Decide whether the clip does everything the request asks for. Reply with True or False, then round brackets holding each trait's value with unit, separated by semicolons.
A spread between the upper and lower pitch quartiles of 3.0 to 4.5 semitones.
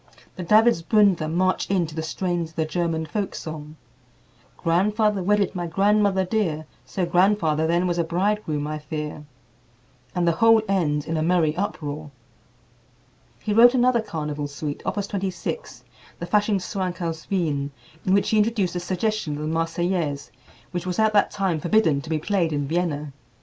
True (4.2 semitones)